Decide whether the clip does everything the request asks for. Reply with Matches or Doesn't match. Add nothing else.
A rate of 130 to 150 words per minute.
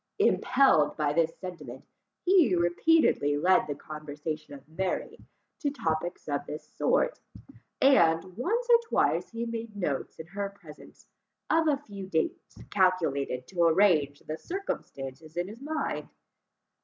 Matches